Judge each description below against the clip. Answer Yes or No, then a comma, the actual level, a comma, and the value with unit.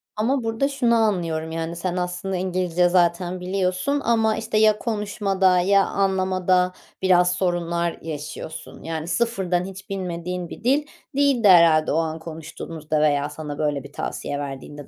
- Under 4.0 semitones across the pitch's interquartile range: Yes, average, 3.4 semitones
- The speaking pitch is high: No, medium, 180 Hz